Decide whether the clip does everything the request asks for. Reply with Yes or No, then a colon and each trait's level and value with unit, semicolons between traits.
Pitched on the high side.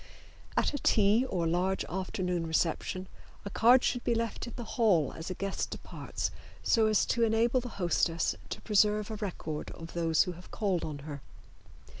Yes: high, 195 Hz